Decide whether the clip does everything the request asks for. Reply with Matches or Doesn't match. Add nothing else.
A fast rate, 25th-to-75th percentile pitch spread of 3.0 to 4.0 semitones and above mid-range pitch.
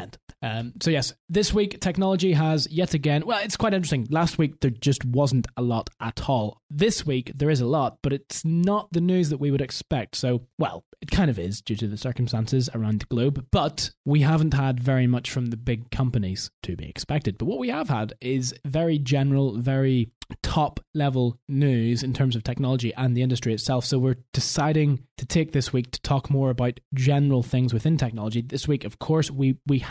Doesn't match